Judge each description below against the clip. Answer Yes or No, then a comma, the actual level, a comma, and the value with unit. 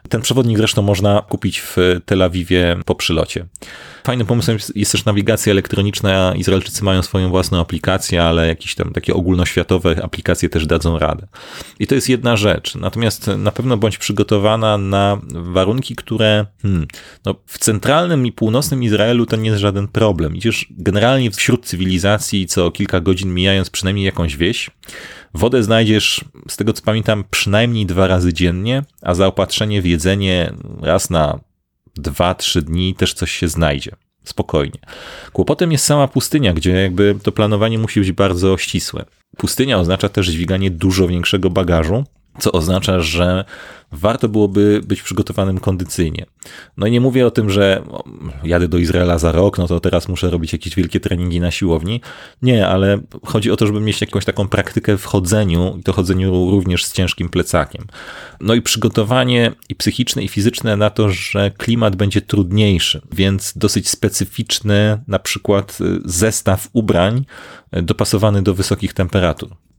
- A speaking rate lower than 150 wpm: No, average, 155 wpm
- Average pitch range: Yes, average, 3.1 semitones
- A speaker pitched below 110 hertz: Yes, low, 100 Hz